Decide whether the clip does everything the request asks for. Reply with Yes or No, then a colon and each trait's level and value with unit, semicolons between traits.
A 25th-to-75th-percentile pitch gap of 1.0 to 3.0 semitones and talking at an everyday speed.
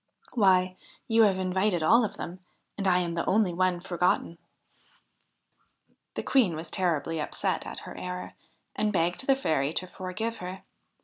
Yes: narrow, 2.5 semitones; average, 160 wpm